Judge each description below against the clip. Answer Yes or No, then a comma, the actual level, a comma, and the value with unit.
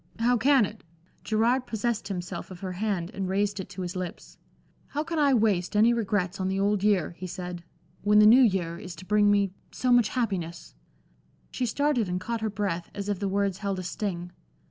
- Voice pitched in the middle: No, high, 200 Hz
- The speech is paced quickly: Yes, fast, 210 wpm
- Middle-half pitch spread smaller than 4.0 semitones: Yes, average, 3.3 semitones